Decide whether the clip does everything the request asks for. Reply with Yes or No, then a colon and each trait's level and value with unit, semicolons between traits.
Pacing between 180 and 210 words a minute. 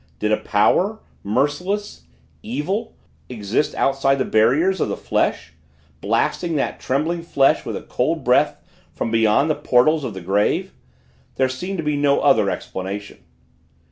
No: average, 145 wpm